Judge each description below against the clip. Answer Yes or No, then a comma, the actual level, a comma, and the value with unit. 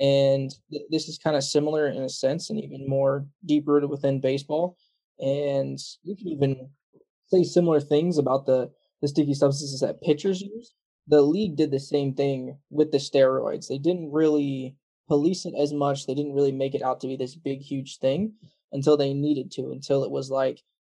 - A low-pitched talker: No, medium, 145 Hz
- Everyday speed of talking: Yes, average, 195 wpm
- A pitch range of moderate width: No, narrow, 2.2 semitones